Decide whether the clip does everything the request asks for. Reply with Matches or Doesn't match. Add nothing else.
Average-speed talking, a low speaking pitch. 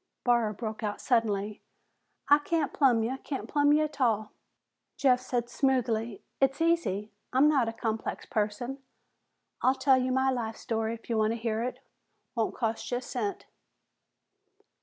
Doesn't match